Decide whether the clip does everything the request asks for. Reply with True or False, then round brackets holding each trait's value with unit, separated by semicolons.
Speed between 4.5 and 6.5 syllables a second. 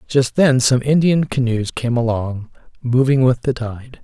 False (4.3 syllables/s)